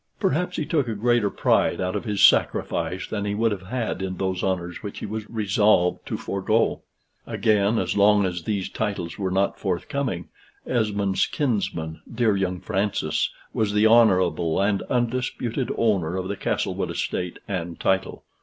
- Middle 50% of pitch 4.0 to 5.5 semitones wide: No, average, 3.2 semitones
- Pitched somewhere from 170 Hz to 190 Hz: No, low, 100 Hz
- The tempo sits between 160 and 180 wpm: Yes, average, 165 wpm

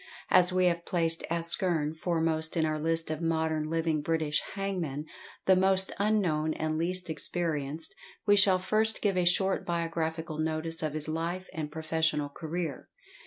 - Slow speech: No, average, 155 wpm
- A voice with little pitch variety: Yes, narrow, 2.3 semitones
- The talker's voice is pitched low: No, medium, 165 Hz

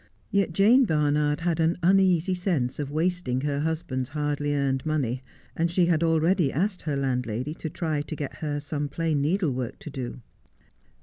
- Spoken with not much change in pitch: No, average, 3.3 semitones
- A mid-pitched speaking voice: Yes, medium, 155 Hz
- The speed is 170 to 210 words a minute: Yes, average, 175 wpm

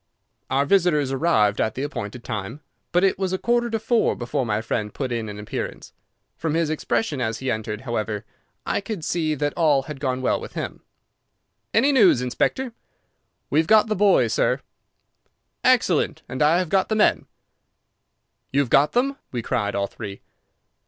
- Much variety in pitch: Yes, wide, 8.1 semitones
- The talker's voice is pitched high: No, medium, 145 Hz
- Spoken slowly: No, average, 180 wpm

